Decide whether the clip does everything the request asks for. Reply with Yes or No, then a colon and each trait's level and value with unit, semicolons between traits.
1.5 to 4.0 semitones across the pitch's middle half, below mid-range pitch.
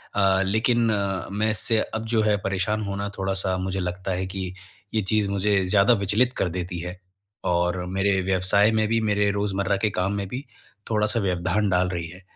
Yes: narrow, 2.4 semitones; low, 100 Hz